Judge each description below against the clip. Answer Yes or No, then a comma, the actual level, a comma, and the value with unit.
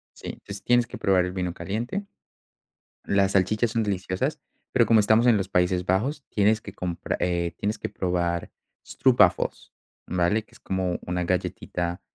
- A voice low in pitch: Yes, very low, 95 Hz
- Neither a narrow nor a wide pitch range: Yes, average, 3.3 semitones